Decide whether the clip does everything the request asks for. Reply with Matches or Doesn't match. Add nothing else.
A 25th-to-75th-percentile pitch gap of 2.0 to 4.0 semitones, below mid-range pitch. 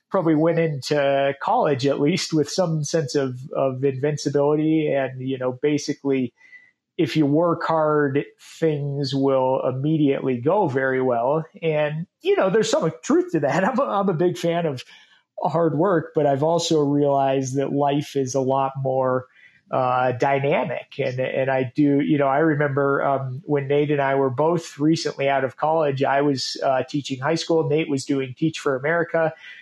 Doesn't match